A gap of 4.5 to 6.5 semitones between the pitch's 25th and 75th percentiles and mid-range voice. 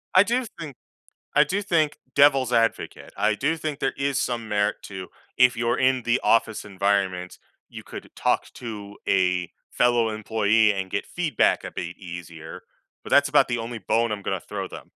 No: average, 5.2 semitones; low, 115 Hz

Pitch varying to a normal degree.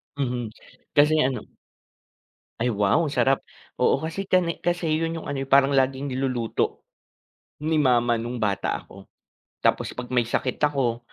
Yes: average, 3.8 semitones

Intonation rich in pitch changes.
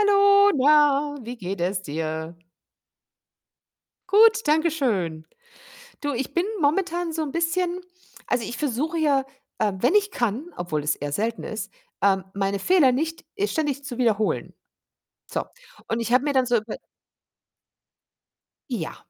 Yes: wide, 8.1 semitones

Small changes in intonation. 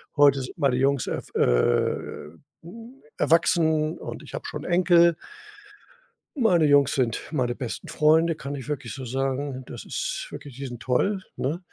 No: average, 4.2 semitones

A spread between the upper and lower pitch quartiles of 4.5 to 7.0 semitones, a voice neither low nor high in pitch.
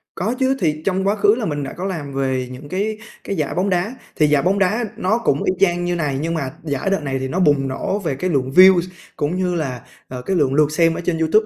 Yes: average, 5.1 semitones; medium, 170 Hz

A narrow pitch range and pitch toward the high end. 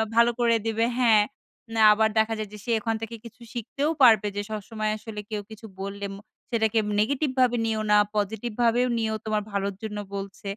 Yes: narrow, 1.9 semitones; high, 220 Hz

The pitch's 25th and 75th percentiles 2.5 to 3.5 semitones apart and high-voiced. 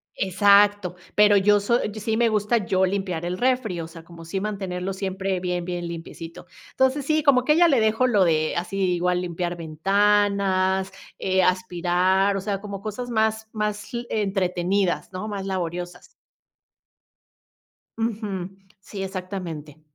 Yes: average, 2.8 semitones; high, 195 Hz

